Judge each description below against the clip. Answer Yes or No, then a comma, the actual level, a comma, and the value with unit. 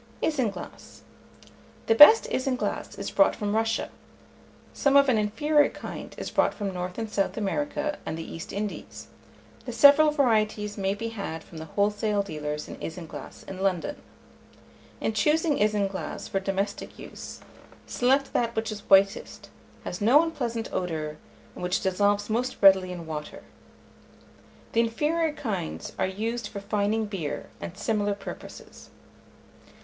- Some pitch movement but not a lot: Yes, average, 4.2 semitones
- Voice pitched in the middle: No, high, 210 Hz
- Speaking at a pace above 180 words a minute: No, average, 145 wpm